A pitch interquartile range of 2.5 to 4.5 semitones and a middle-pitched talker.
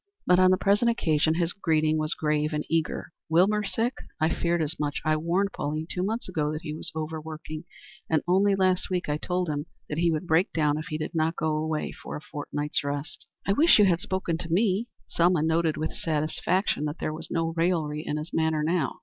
Yes: average, 2.8 semitones; medium, 160 Hz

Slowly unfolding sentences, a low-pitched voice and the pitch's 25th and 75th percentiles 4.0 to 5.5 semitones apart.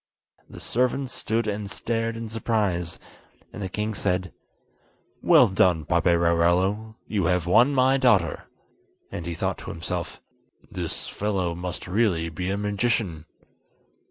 Yes: slow, 130 wpm; very low, 95 Hz; average, 4.3 semitones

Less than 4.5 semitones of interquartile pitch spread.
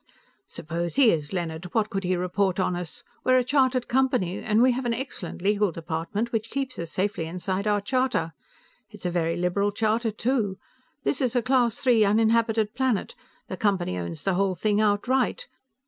No: average, 5.0 semitones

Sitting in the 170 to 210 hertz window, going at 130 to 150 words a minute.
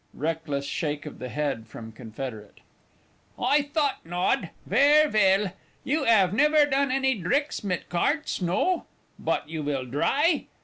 Yes: high, 190 Hz; average, 140 wpm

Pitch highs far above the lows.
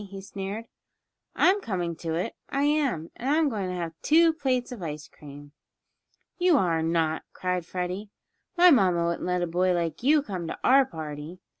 Yes: wide, 8.0 semitones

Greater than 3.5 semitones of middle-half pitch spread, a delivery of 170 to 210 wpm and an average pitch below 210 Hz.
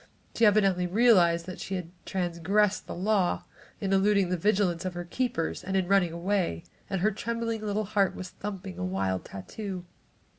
No: average, 3.0 semitones; average, 175 wpm; high, 190 Hz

